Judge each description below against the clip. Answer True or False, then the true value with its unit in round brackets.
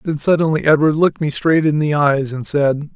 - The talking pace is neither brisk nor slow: False (225 wpm)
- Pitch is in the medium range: True (150 Hz)